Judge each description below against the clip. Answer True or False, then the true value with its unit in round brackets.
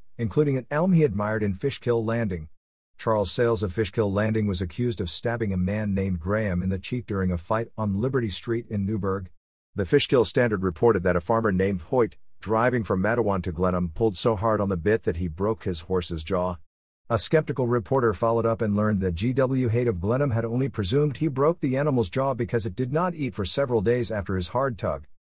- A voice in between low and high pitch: False (110 Hz)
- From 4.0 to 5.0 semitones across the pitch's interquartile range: True (4.3 semitones)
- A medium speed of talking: False (215 wpm)